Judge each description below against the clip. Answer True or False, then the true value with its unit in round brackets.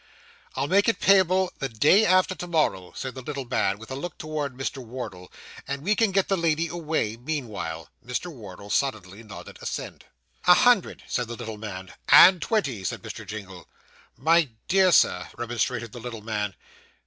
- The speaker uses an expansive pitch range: True (8.0 semitones)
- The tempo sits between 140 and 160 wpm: False (175 wpm)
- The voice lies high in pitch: False (130 Hz)